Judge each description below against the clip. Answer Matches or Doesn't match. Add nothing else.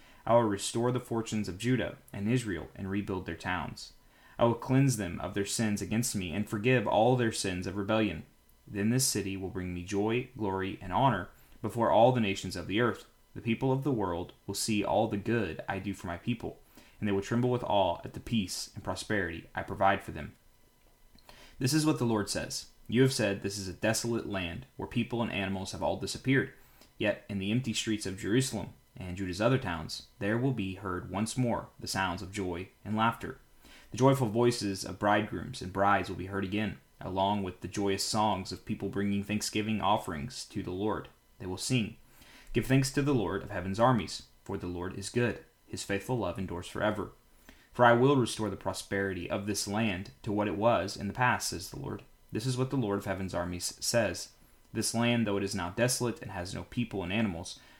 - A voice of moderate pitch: Doesn't match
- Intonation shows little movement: Doesn't match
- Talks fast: Matches